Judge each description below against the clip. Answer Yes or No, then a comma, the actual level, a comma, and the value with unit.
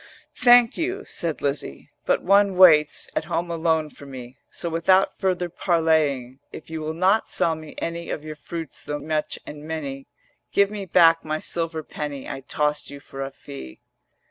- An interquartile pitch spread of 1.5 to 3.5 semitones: Yes, average, 2.9 semitones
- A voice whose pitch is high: No, medium, 160 Hz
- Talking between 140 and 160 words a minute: No, average, 175 wpm